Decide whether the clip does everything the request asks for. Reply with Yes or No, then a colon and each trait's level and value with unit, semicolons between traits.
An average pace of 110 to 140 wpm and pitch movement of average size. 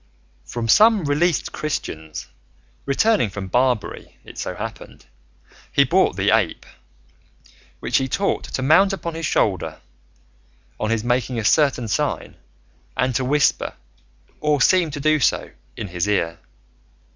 No: slow, 135 wpm; wide, 6.1 semitones